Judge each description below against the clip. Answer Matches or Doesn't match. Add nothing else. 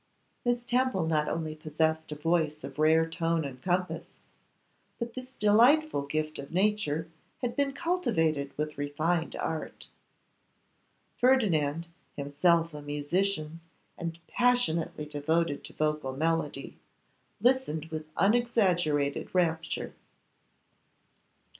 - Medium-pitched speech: Matches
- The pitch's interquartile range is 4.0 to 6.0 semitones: Matches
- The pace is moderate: Doesn't match